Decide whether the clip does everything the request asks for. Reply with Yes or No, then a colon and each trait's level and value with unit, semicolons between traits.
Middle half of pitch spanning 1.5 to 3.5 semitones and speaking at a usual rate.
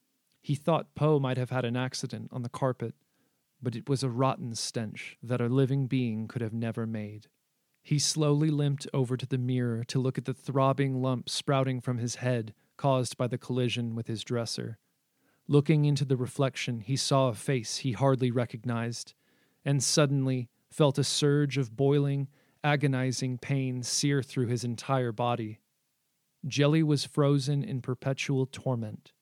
Yes: narrow, 2.4 semitones; average, 165 wpm